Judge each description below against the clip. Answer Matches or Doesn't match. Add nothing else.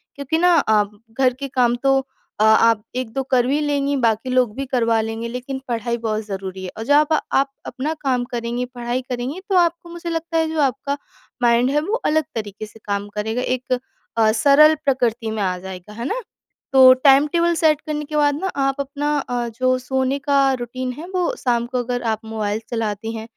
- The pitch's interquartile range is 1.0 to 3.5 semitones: Doesn't match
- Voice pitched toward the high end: Matches